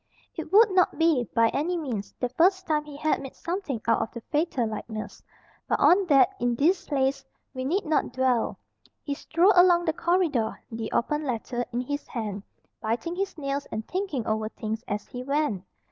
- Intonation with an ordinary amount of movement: No, wide, 6.5 semitones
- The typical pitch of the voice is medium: No, very high, 275 Hz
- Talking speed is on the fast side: No, average, 190 wpm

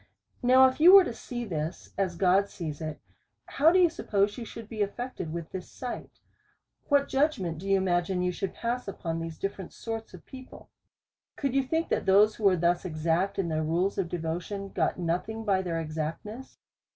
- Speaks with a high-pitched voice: Yes, high, 195 Hz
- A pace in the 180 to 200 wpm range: Yes, average, 195 wpm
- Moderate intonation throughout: No, wide, 5.8 semitones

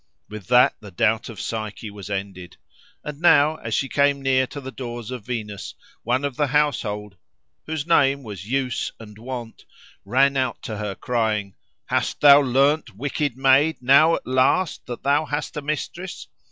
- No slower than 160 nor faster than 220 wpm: Yes, average, 170 wpm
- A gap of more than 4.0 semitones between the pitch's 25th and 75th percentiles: Yes, average, 4.7 semitones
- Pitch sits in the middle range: No, low, 130 Hz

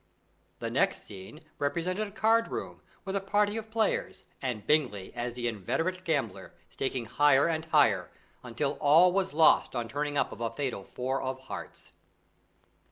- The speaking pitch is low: No, medium, 145 Hz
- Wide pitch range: Yes, wide, 7.2 semitones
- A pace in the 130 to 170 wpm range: Yes, average, 165 wpm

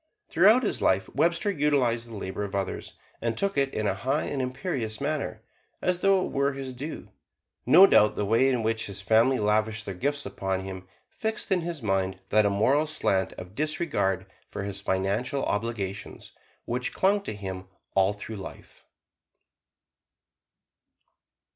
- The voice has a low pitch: Yes, low, 115 Hz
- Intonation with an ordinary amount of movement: No, wide, 6.6 semitones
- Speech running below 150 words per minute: No, average, 160 wpm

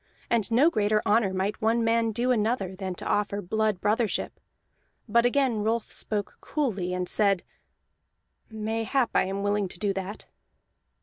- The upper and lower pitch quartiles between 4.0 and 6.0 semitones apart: No, narrow, 2.6 semitones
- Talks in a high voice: Yes, high, 215 Hz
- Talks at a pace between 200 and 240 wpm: No, average, 150 wpm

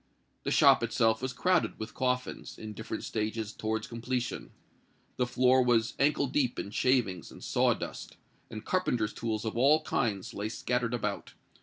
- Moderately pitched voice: No, low, 115 Hz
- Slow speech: No, average, 155 wpm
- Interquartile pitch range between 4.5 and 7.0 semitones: No, narrow, 2.6 semitones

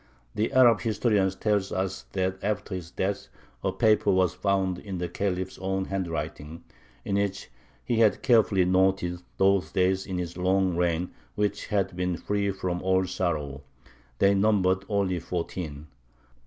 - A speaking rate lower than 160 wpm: Yes, average, 150 wpm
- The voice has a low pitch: Yes, very low, 95 Hz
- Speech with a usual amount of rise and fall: No, narrow, 1.9 semitones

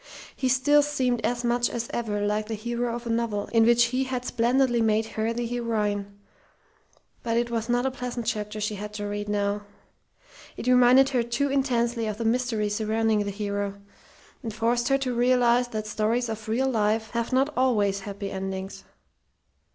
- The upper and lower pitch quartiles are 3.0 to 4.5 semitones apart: No, narrow, 2.6 semitones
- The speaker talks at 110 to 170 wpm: No, average, 180 wpm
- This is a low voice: No, high, 230 Hz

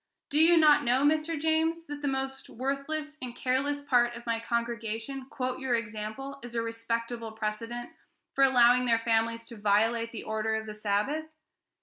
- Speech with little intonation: No, average, 3.4 semitones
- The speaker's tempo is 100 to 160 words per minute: No, average, 175 wpm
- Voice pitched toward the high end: Yes, high, 240 Hz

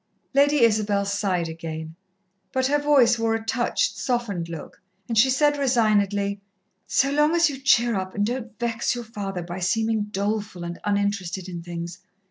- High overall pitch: Yes, high, 215 Hz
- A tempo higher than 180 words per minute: No, average, 165 wpm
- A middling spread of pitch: Yes, average, 4.4 semitones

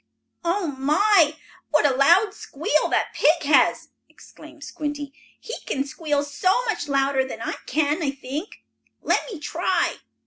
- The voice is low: No, very high, 295 Hz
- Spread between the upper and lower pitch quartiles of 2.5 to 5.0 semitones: Yes, average, 3.5 semitones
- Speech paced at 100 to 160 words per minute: Yes, average, 140 wpm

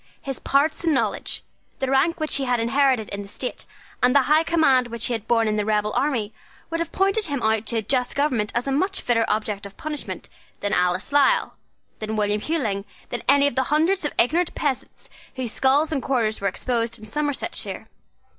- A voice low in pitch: No, very high, 255 Hz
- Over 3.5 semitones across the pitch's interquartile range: Yes, average, 5.0 semitones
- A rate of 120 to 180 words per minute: No, fast, 205 wpm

